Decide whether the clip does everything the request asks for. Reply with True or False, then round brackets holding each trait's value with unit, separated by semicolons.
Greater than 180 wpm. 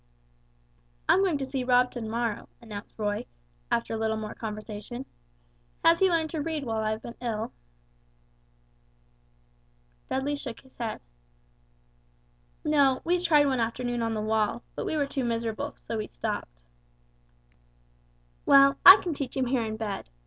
False (155 wpm)